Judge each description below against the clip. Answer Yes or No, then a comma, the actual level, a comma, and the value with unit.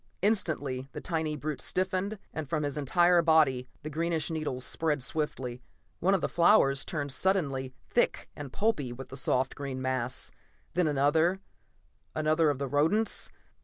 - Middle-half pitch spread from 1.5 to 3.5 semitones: No, average, 4.0 semitones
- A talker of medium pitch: Yes, medium, 150 Hz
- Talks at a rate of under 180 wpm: Yes, average, 155 wpm